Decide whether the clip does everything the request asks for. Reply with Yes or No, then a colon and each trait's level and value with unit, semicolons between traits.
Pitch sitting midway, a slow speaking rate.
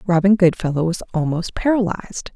Yes: medium, 180 Hz; slow, 125 wpm